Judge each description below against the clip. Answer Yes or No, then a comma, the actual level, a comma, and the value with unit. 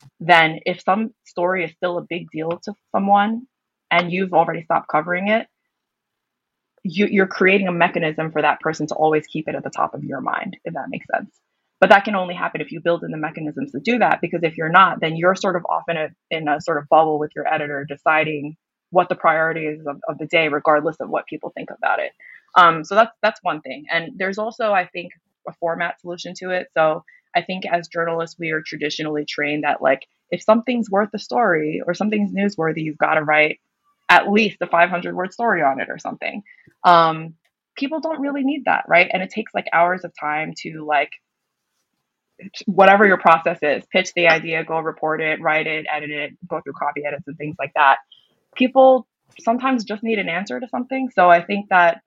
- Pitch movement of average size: Yes, average, 4.1 semitones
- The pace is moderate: No, fast, 215 wpm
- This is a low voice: No, medium, 170 Hz